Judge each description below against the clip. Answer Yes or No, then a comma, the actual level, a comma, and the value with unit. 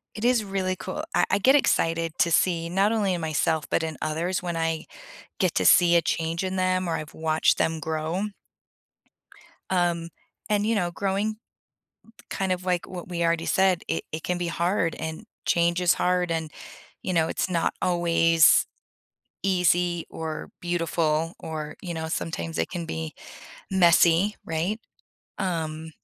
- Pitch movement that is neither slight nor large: No, narrow, 2.2 semitones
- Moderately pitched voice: Yes, medium, 170 Hz